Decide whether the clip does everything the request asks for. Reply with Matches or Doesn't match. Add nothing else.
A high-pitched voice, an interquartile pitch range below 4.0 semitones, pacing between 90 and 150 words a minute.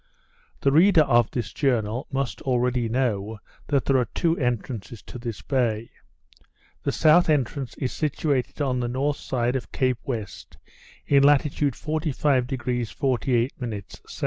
Doesn't match